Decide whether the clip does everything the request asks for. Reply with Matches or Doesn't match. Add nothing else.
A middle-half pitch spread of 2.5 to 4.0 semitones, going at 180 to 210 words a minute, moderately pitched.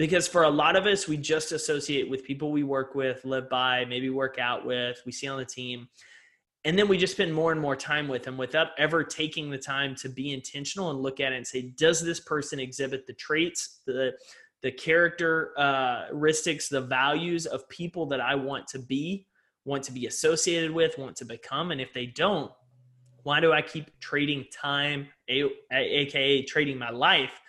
Matches